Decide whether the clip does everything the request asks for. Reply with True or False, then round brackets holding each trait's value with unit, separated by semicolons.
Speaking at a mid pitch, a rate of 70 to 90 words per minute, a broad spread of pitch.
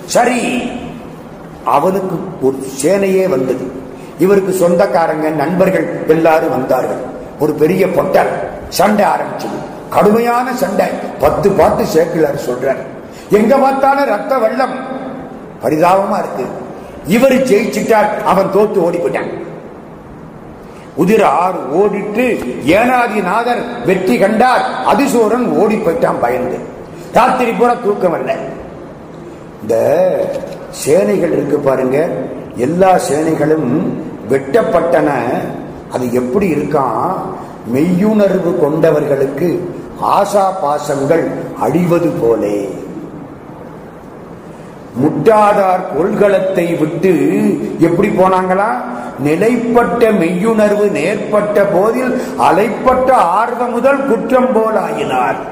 False (195 Hz; 80 wpm; 6.0 semitones)